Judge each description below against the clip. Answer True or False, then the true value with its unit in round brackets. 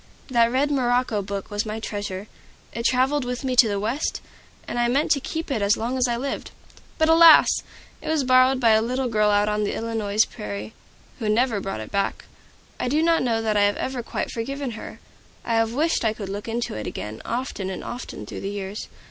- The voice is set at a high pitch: True (230 Hz)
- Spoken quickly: True (220 wpm)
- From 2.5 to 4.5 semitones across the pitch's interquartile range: True (3.8 semitones)